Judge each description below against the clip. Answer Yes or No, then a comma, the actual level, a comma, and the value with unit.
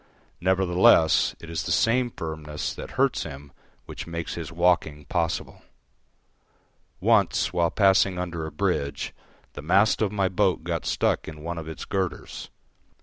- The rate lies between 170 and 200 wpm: No, average, 145 wpm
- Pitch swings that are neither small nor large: Yes, average, 3.1 semitones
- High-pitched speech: No, very low, 85 Hz